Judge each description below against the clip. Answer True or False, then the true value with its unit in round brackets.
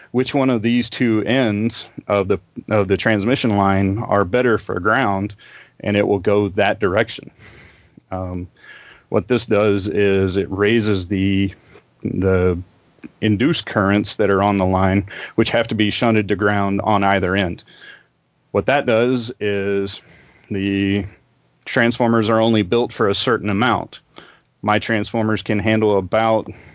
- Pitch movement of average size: False (2.3 semitones)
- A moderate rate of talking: True (150 wpm)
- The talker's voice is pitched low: True (105 Hz)